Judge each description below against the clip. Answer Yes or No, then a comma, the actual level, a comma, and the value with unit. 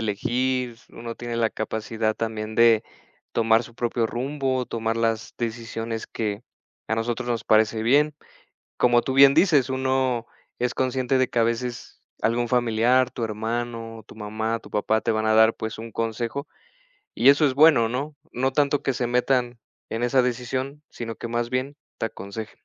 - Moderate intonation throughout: No, narrow, 2.3 semitones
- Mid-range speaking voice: No, low, 120 Hz